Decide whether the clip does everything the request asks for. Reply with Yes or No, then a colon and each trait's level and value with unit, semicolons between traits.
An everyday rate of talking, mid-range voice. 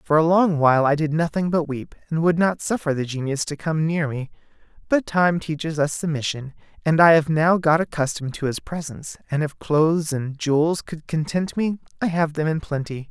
No: fast, 210 wpm; medium, 155 Hz